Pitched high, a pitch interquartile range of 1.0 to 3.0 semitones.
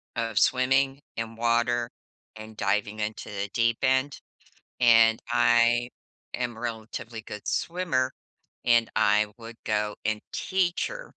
No: low, 115 Hz; narrow, 2.5 semitones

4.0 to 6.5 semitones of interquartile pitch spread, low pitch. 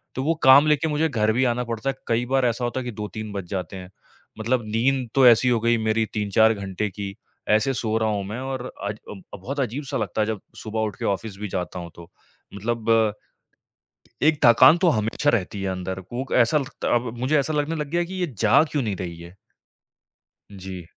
Yes: average, 4.3 semitones; low, 115 Hz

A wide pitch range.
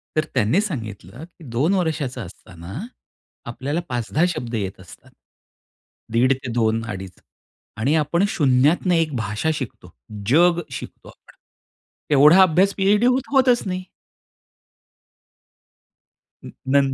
Yes: wide, 7.2 semitones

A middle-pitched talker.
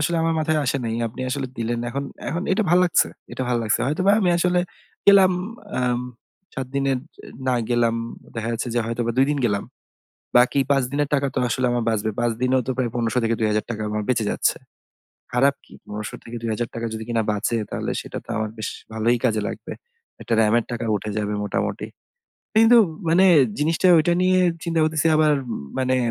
No: low, 125 Hz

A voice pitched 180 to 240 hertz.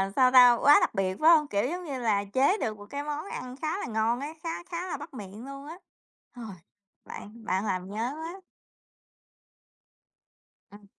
No: very high, 255 Hz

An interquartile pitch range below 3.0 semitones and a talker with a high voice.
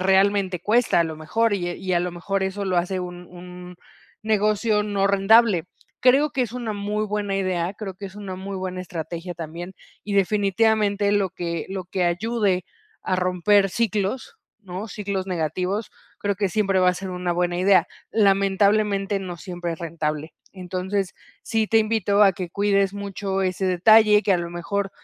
Yes: narrow, 2.4 semitones; high, 195 Hz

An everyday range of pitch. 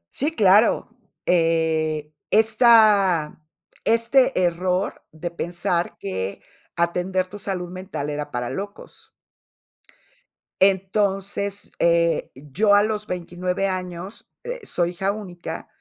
Yes: average, 3.1 semitones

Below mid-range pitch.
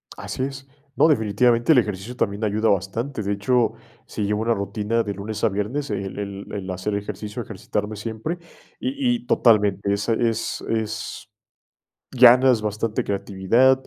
Yes: low, 110 Hz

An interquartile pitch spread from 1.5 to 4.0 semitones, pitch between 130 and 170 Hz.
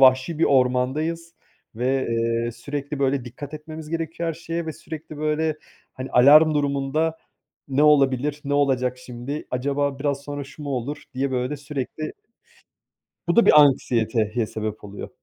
Yes: average, 3.1 semitones; medium, 140 Hz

